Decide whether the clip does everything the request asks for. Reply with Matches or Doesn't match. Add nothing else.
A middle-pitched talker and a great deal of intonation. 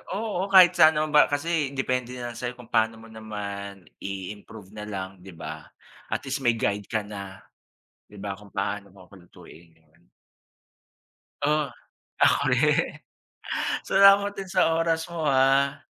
Doesn't match